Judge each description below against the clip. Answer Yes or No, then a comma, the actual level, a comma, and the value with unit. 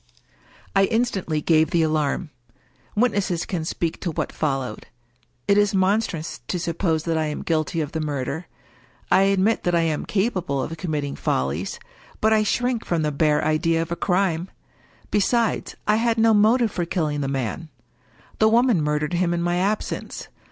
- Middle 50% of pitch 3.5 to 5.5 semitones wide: Yes, average, 4.7 semitones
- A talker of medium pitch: Yes, medium, 170 Hz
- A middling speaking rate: Yes, average, 175 wpm